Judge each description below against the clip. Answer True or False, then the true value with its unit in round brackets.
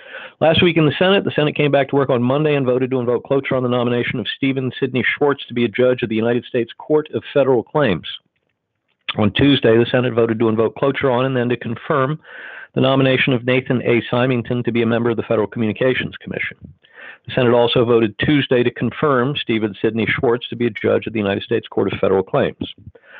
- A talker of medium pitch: False (125 Hz)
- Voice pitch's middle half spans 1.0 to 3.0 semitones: True (2.7 semitones)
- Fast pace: True (225 wpm)